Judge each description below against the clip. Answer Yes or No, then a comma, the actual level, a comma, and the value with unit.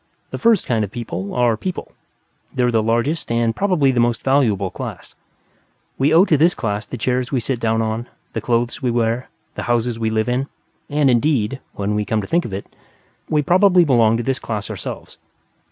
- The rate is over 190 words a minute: Yes, average, 200 wpm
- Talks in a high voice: No, low, 120 Hz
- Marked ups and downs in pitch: No, average, 3.6 semitones